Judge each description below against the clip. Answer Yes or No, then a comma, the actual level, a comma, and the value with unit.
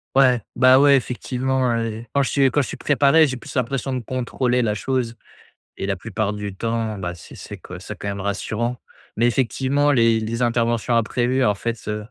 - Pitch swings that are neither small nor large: Yes, average, 3.0 semitones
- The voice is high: No, low, 120 Hz